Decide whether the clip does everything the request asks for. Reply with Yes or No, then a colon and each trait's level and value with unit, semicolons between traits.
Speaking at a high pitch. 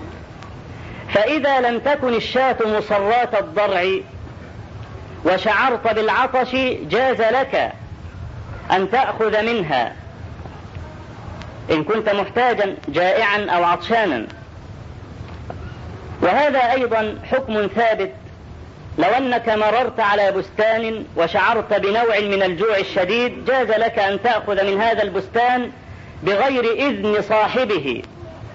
Yes: high, 215 Hz